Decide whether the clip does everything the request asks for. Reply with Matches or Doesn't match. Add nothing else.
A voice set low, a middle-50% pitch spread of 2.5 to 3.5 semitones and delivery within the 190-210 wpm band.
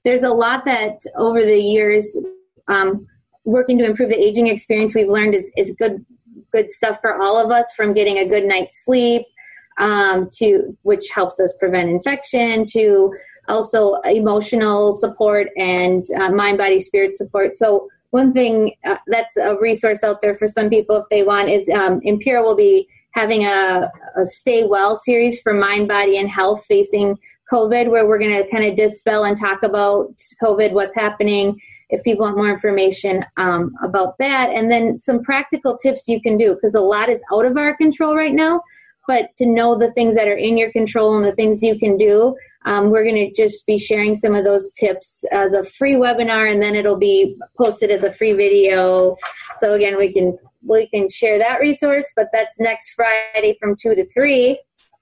Doesn't match